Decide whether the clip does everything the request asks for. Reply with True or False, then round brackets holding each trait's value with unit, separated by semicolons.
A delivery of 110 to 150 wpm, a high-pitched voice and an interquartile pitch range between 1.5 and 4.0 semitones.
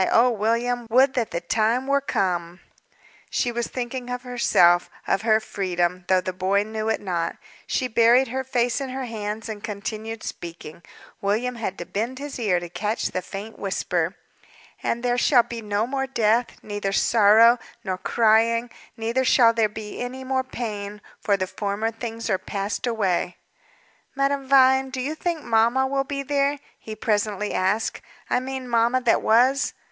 False (170 wpm; 225 Hz; 3.7 semitones)